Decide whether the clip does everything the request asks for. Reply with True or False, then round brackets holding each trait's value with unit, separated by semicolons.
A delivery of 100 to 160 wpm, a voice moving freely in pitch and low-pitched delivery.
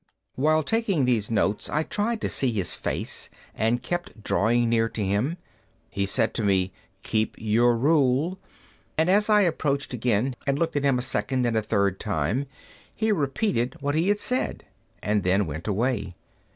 False (175 wpm; 6.6 semitones; 125 Hz)